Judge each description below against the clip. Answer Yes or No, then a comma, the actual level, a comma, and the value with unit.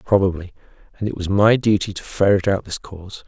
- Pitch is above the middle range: No, low, 100 Hz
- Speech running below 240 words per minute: Yes, average, 200 wpm